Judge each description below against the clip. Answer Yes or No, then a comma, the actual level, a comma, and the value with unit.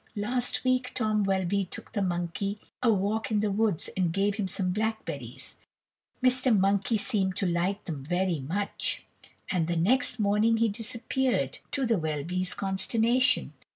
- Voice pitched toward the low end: No, high, 200 Hz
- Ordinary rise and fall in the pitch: Yes, average, 3.6 semitones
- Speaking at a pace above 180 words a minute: No, average, 155 wpm